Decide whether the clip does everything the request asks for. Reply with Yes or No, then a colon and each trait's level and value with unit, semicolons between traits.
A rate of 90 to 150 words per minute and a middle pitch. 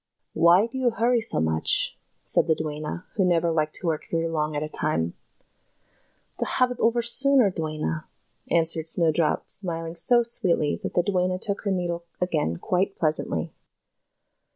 No: average, 170 wpm; medium, 170 Hz